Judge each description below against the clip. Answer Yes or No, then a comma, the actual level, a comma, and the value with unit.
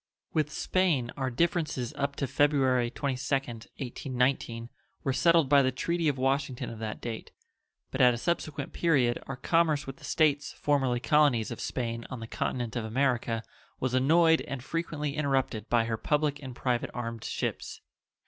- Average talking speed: Yes, average, 165 wpm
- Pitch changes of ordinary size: Yes, average, 3.5 semitones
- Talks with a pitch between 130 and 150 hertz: Yes, low, 135 Hz